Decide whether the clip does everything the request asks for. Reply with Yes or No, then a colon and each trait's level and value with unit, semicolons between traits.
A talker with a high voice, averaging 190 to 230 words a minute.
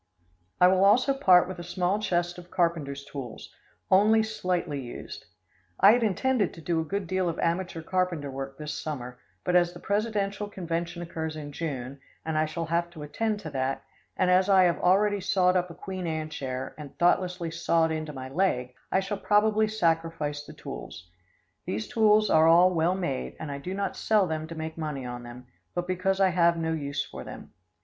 No: medium, 170 Hz; average, 200 wpm